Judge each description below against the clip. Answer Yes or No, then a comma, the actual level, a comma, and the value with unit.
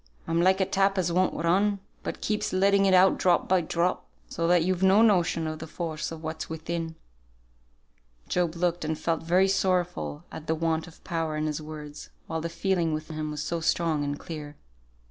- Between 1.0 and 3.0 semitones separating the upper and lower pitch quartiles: Yes, narrow, 2.6 semitones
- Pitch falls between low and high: Yes, medium, 170 Hz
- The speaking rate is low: No, average, 200 wpm